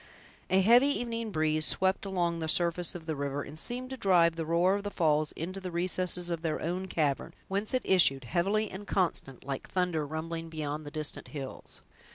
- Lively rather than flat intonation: No, average, 3.5 semitones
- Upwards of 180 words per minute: Yes, average, 200 wpm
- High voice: No, medium, 170 Hz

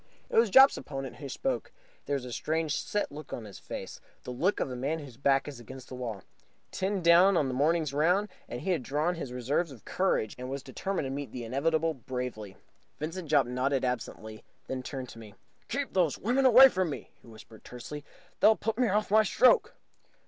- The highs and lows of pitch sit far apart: Yes, wide, 6.2 semitones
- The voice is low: No, medium, 145 Hz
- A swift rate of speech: Yes, fast, 210 wpm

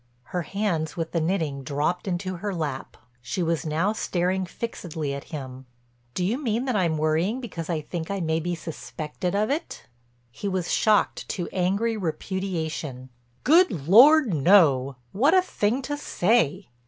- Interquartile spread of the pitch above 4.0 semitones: Yes, average, 4.7 semitones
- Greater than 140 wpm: Yes, average, 160 wpm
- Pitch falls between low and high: Yes, medium, 175 Hz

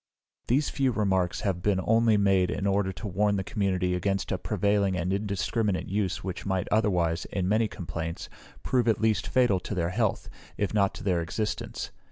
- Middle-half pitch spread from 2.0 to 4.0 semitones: Yes, average, 2.7 semitones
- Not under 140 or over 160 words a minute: No, average, 185 wpm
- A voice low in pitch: Yes, low, 100 Hz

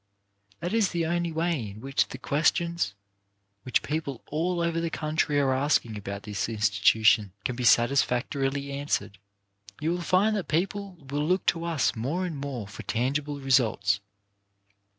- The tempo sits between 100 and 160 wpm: Yes, average, 155 wpm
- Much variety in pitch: Yes, wide, 6.1 semitones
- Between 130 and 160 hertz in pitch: Yes, medium, 140 Hz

